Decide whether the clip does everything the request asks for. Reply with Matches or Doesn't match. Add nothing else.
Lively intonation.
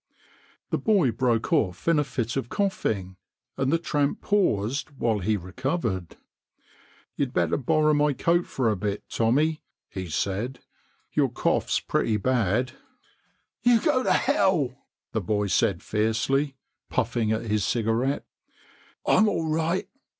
Matches